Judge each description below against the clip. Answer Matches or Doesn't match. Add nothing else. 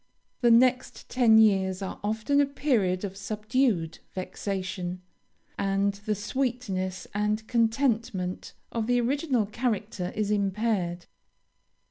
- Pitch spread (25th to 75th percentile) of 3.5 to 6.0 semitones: Matches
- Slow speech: Matches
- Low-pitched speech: Doesn't match